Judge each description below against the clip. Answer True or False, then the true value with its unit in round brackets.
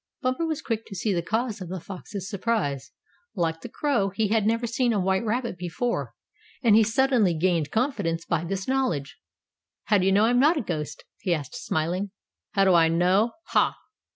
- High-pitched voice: True (200 Hz)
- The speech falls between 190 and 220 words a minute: True (195 wpm)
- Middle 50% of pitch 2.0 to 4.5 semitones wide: False (5.0 semitones)